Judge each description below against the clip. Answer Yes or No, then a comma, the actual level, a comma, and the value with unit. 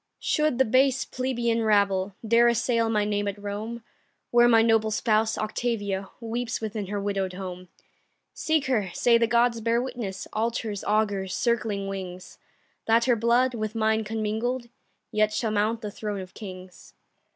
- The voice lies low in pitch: No, high, 220 Hz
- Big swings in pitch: No, narrow, 2.6 semitones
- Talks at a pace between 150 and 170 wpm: Yes, average, 155 wpm